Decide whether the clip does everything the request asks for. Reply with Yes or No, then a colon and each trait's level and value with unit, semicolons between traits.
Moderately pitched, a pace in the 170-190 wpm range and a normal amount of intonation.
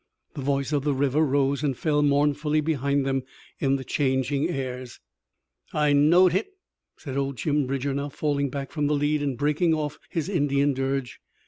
No: medium, 145 Hz; average, 180 wpm; narrow, 1.6 semitones